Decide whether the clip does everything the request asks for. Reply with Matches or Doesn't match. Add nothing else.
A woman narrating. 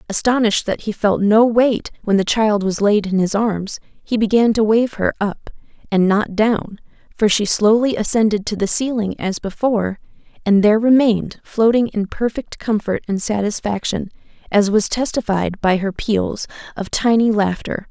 Matches